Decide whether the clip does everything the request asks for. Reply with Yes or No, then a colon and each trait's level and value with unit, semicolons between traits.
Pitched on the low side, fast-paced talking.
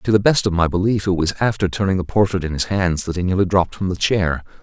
Yes: very low, 95 Hz; fast, 285 wpm